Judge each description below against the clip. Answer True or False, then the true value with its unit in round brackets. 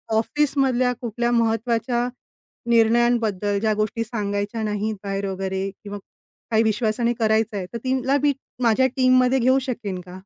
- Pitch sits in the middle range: False (225 Hz)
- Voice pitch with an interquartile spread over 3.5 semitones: False (3.2 semitones)